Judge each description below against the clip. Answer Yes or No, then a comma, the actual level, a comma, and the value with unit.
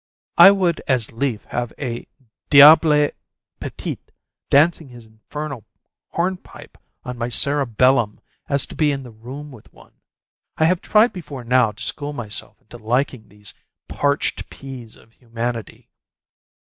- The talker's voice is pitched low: Yes, low, 130 Hz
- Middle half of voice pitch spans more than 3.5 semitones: Yes, average, 4.1 semitones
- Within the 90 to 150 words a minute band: Yes, slow, 135 wpm